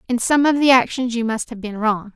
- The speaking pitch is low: No, high, 235 Hz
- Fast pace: Yes, fast, 280 wpm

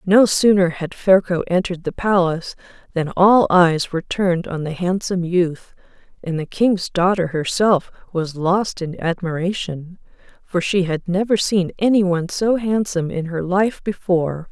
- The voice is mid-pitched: Yes, medium, 180 Hz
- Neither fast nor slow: Yes, average, 155 wpm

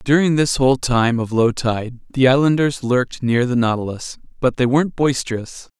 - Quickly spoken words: No, average, 175 wpm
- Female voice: No, male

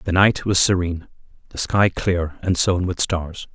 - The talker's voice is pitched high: No, very low, 90 Hz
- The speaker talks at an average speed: Yes, average, 185 wpm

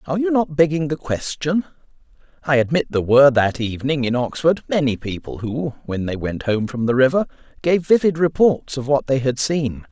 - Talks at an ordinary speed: Yes, average, 195 wpm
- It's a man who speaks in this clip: Yes, male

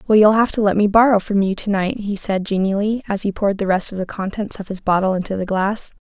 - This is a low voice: No, high, 200 Hz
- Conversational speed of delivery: No, fast, 280 wpm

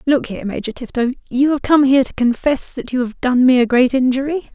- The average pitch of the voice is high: Yes, very high, 260 Hz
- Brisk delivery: Yes, fast, 240 wpm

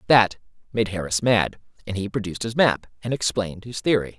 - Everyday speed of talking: Yes, average, 185 wpm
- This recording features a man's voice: Yes, male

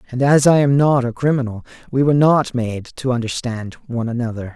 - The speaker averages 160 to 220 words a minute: Yes, average, 200 wpm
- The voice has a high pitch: No, low, 125 Hz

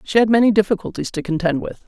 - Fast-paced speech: Yes, fast, 225 wpm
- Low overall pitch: No, high, 200 Hz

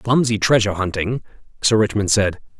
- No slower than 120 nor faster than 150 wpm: Yes, average, 140 wpm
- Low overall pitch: Yes, low, 105 Hz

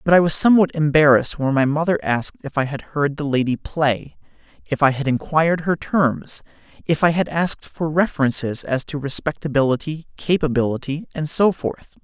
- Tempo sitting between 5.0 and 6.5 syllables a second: Yes, 5.4 syllables/s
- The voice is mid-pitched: Yes, medium, 150 Hz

